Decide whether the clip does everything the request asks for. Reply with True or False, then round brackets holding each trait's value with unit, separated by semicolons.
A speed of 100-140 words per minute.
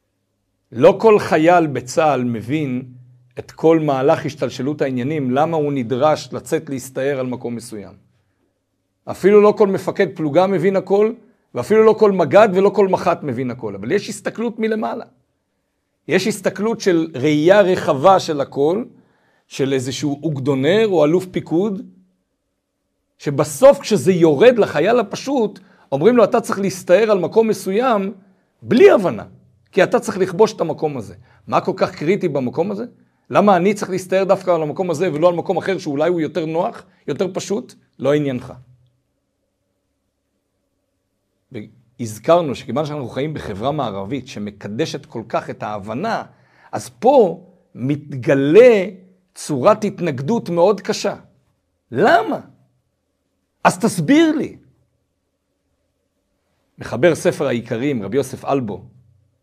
True (130 wpm)